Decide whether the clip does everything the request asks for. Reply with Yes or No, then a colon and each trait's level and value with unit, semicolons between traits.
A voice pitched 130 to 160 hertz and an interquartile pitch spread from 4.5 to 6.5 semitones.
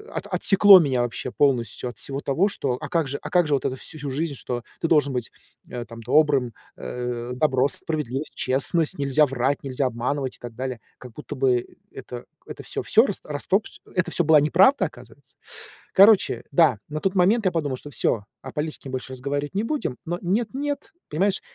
Yes: medium, 140 Hz; average, 4.8 semitones